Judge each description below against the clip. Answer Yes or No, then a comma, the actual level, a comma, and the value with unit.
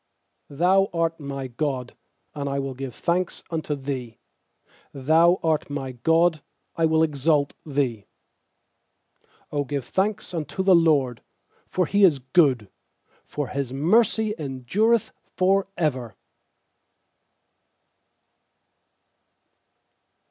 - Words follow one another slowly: Yes, slow, 105 wpm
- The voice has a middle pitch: Yes, medium, 150 Hz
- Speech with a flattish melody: No, average, 4.3 semitones